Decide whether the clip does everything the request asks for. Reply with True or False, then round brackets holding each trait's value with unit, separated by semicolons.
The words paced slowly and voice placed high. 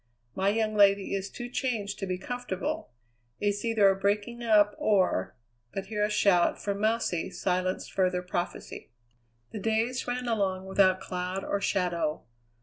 False (155 wpm; 200 Hz)